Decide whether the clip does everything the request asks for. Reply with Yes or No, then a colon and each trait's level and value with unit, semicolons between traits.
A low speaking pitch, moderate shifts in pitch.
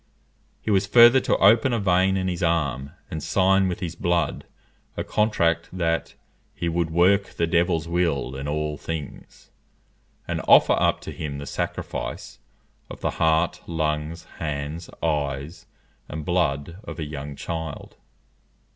Yes: very low, 85 Hz; average, 3.1 semitones